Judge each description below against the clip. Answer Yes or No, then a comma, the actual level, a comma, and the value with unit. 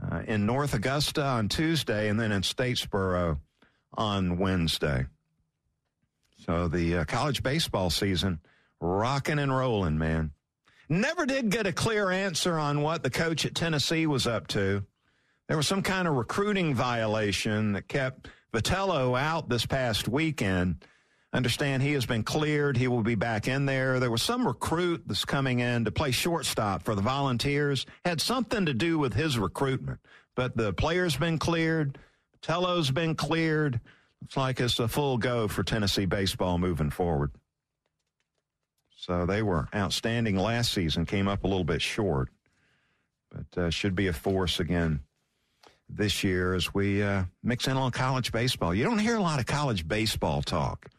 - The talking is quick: No, average, 165 wpm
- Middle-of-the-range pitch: No, low, 120 Hz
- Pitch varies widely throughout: Yes, wide, 6.9 semitones